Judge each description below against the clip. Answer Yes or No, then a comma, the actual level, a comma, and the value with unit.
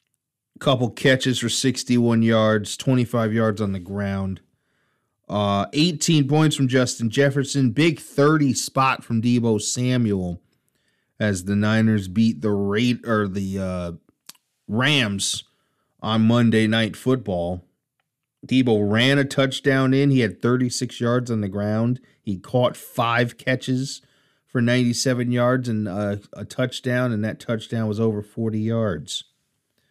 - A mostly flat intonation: No, average, 3.5 semitones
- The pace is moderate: No, slow, 130 wpm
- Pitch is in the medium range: No, low, 120 Hz